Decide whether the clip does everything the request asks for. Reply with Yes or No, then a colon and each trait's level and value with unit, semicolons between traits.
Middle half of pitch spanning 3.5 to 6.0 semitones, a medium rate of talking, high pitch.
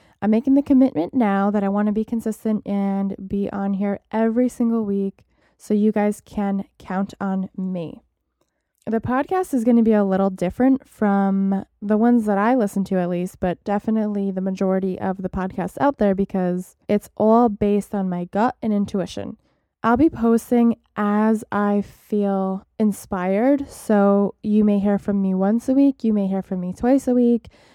No: average, 2.7 semitones; average, 185 wpm; high, 205 Hz